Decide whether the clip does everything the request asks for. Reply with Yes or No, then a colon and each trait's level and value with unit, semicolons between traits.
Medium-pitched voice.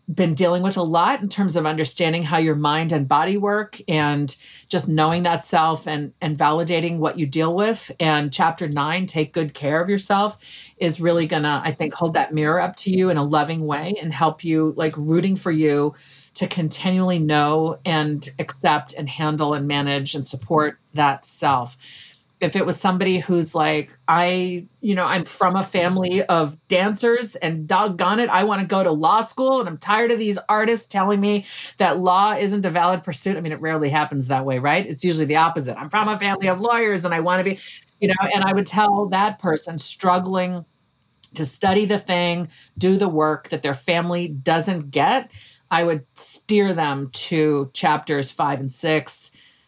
Yes: medium, 170 Hz